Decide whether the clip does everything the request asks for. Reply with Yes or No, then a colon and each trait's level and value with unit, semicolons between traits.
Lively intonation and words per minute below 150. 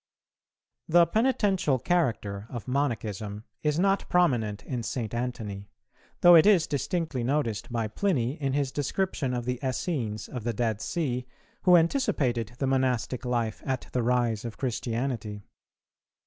No: average, 4.8 semitones; average, 140 wpm